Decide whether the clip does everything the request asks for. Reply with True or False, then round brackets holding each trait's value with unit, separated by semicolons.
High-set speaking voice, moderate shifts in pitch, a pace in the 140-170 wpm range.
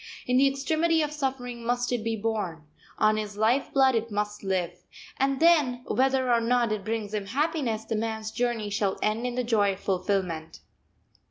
False (230 Hz; 3.7 semitones; 185 wpm)